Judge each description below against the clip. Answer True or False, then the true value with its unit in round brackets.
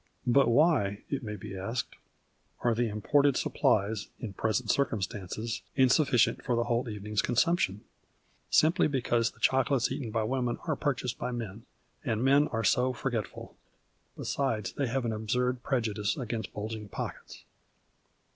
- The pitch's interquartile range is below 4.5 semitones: True (3.6 semitones)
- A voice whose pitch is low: True (120 Hz)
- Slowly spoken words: False (145 wpm)